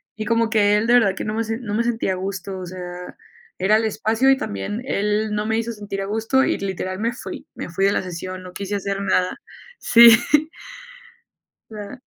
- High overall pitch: Yes, high, 210 Hz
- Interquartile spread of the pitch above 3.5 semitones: No, average, 2.9 semitones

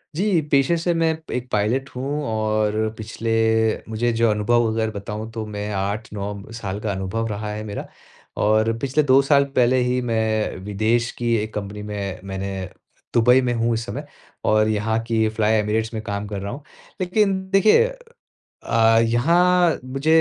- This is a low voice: Yes, low, 110 Hz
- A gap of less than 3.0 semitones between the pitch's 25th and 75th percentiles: No, average, 3.4 semitones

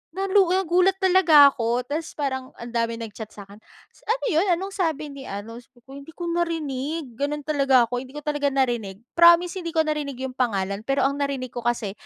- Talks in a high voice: Yes, very high, 280 Hz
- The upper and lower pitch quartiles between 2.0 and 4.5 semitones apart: No, average, 5.3 semitones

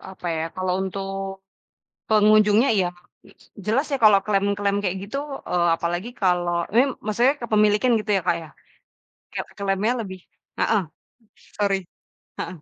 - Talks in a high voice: Yes, high, 200 Hz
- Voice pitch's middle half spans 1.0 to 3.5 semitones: Yes, narrow, 2.4 semitones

